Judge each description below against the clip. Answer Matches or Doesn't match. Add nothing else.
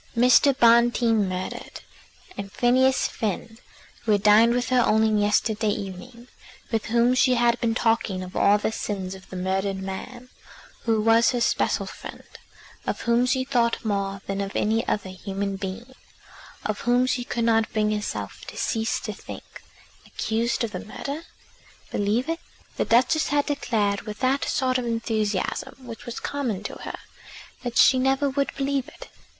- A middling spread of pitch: Matches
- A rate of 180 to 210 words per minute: Doesn't match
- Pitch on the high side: Matches